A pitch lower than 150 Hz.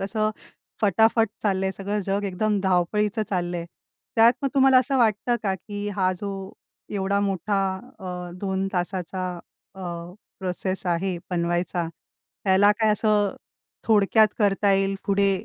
No: high, 195 Hz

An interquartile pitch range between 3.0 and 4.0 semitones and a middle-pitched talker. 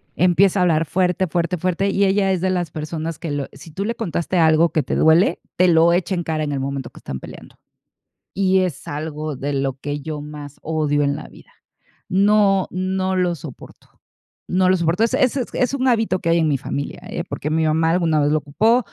Yes: average, 3.6 semitones; medium, 170 Hz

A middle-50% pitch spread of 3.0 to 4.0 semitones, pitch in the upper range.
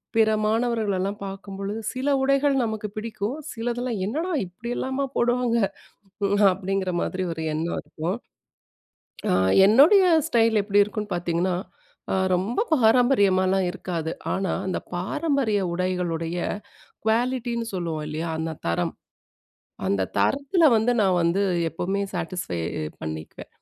No: average, 4.9 semitones; high, 200 Hz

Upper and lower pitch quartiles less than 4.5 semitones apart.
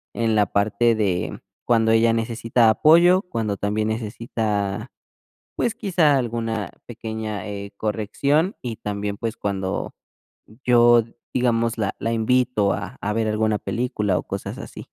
Yes: narrow, 2.4 semitones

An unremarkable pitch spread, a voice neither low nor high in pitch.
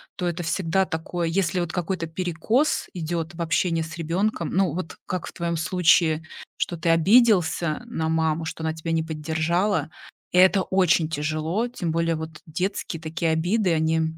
No: narrow, 2.2 semitones; medium, 165 Hz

